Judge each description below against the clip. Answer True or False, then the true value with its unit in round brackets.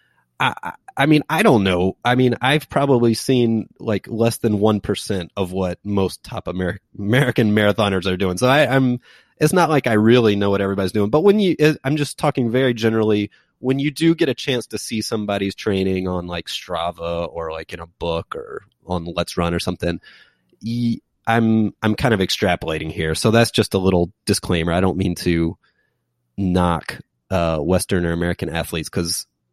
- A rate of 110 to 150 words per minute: False (190 wpm)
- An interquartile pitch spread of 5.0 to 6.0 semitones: True (5.3 semitones)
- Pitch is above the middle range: False (100 Hz)